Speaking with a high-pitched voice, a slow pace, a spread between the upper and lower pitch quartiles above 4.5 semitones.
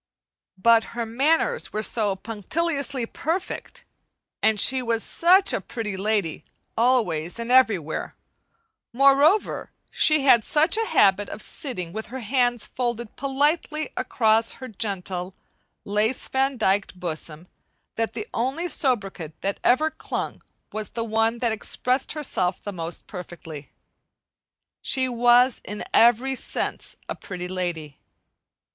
Yes: high, 230 Hz; slow, 125 wpm; average, 5.2 semitones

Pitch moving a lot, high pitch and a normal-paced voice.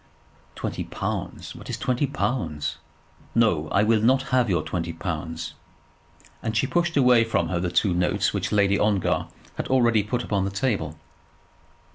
No: wide, 5.9 semitones; low, 105 Hz; average, 160 wpm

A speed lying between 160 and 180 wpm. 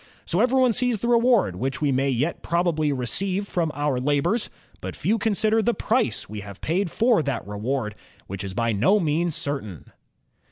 Yes: average, 175 wpm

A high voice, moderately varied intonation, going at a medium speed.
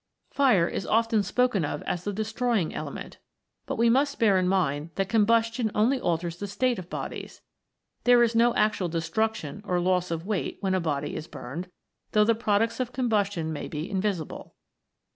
Yes: high, 205 Hz; average, 4.7 semitones; average, 185 wpm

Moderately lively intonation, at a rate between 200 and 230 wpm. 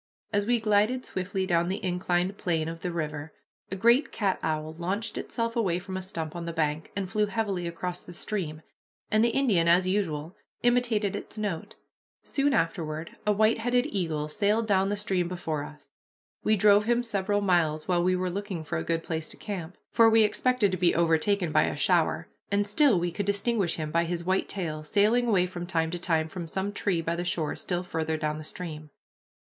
Yes: average, 3.9 semitones; fast, 205 wpm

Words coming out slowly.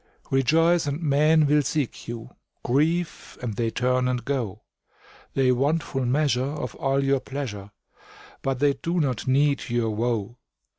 No: average, 150 wpm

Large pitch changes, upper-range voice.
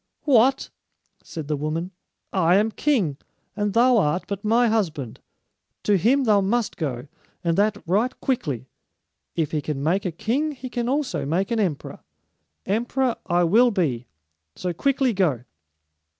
Yes: wide, 6.8 semitones; high, 200 Hz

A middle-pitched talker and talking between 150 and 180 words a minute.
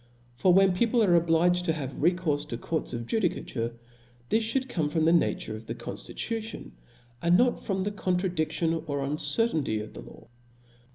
Yes: medium, 170 Hz; average, 175 wpm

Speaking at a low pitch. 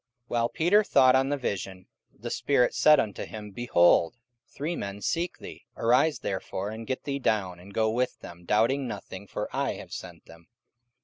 Yes: low, 115 Hz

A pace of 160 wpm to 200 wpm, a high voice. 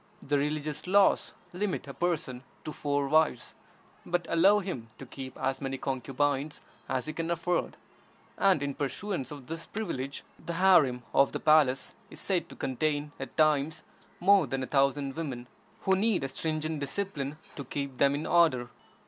No: average, 165 wpm; medium, 145 Hz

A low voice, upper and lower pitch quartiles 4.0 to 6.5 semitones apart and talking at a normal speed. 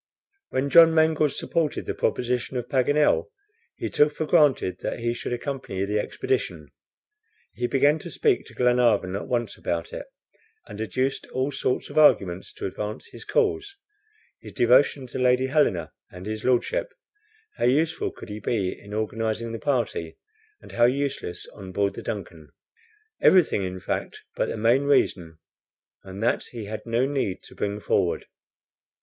Yes: low, 120 Hz; wide, 5.5 semitones; average, 160 wpm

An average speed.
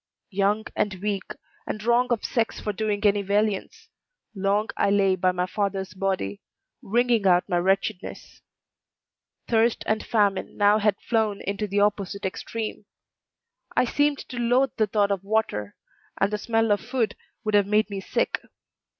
Yes: average, 160 wpm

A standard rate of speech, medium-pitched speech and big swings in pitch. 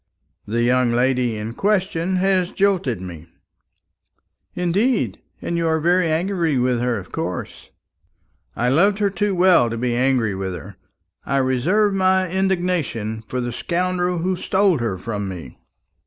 Yes: average, 150 wpm; medium, 160 Hz; wide, 7.8 semitones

